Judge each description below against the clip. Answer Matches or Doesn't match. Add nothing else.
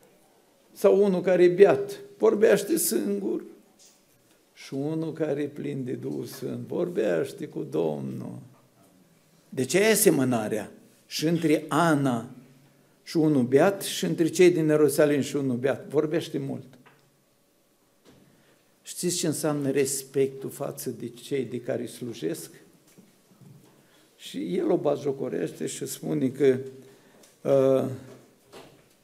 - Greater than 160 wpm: Doesn't match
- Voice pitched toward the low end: Doesn't match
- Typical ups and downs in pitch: Matches